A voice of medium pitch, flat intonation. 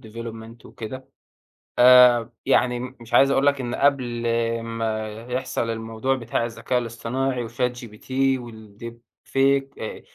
No: low, 120 Hz; narrow, 2.2 semitones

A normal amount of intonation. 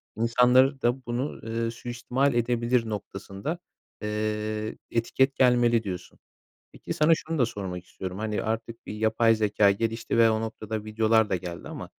No: narrow, 2.1 semitones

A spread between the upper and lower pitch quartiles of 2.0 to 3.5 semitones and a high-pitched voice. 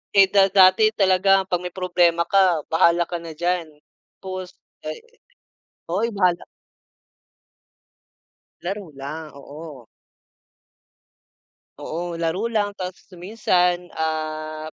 No: average, 2.8 semitones; medium, 180 Hz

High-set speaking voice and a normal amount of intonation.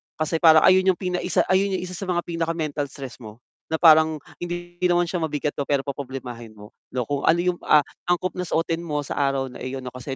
No: medium, 160 Hz; average, 4.3 semitones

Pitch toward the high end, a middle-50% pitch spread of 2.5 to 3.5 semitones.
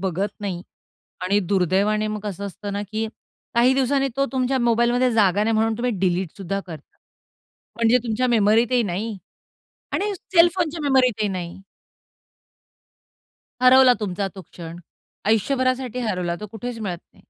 No: high, 215 Hz; average, 4.3 semitones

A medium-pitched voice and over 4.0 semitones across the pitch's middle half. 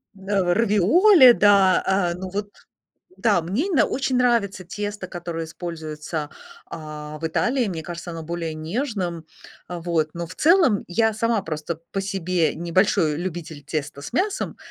Yes: medium, 180 Hz; average, 4.5 semitones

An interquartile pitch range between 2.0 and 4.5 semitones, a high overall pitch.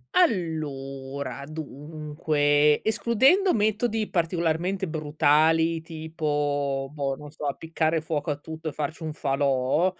No: narrow, 2.4 semitones; medium, 155 Hz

